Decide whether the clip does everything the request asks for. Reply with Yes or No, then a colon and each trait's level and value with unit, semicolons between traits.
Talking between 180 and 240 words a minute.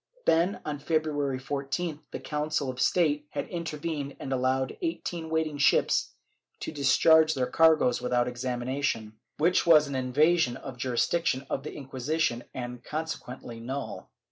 No: average, 155 wpm